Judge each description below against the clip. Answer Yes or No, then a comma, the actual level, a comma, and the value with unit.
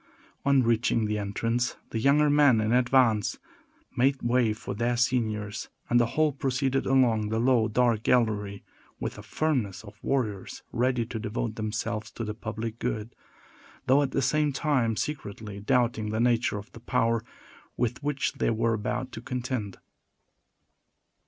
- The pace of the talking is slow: No, average, 155 wpm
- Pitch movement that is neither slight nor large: Yes, average, 3.0 semitones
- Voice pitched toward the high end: No, low, 115 Hz